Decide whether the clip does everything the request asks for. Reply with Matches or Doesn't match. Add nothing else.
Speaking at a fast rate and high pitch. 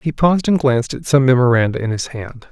Doesn't match